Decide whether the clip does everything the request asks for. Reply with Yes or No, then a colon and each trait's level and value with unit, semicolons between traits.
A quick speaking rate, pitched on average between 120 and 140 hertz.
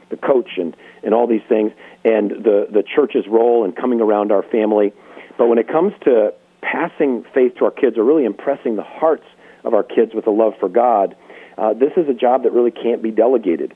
Yes: fast, 220 wpm; low, 125 Hz